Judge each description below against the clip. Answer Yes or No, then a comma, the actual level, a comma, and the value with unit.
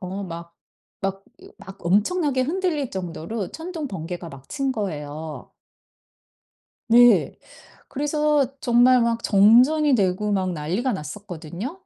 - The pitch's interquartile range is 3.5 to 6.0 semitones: No, wide, 7.0 semitones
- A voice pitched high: Yes, high, 210 Hz